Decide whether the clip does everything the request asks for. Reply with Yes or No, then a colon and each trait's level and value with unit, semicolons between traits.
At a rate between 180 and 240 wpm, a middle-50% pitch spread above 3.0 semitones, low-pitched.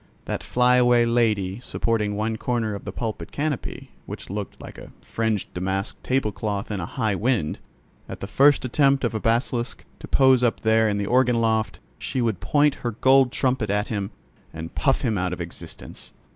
Yes: average, 185 wpm; average, 3.5 semitones; low, 115 Hz